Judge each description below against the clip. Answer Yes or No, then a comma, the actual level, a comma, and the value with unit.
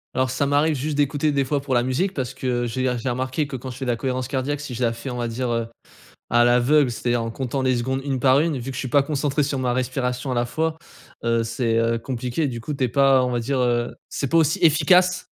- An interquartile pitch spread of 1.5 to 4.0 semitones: Yes, average, 2.8 semitones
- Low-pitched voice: Yes, low, 130 Hz